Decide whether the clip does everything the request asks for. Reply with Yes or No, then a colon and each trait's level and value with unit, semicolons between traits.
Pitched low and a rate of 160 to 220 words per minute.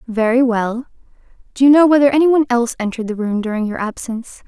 No: high, 245 Hz; average, 200 wpm